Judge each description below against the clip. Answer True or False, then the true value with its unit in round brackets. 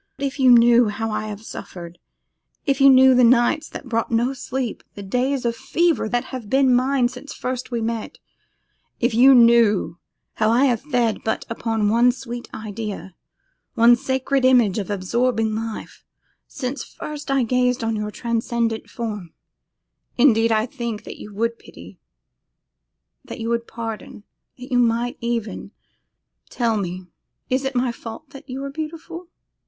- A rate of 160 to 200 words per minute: True (165 wpm)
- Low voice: False (235 Hz)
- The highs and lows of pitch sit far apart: False (2.7 semitones)